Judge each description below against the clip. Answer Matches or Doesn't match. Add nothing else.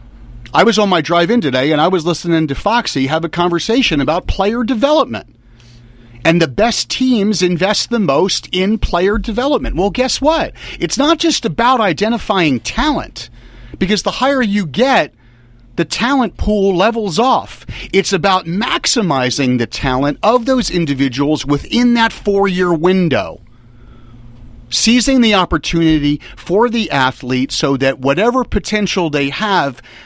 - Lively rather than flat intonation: Matches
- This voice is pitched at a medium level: Matches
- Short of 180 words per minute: Matches